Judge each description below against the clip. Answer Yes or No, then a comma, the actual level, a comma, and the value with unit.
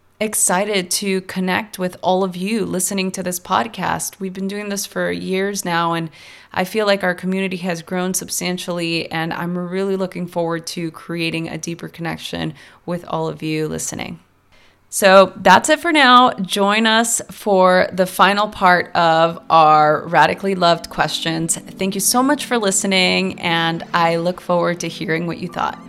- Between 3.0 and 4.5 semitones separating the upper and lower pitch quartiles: No, narrow, 2.6 semitones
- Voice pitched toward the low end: No, medium, 180 Hz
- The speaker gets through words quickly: No, average, 170 wpm